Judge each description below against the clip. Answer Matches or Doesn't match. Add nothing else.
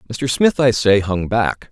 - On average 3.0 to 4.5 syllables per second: Matches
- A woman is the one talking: Doesn't match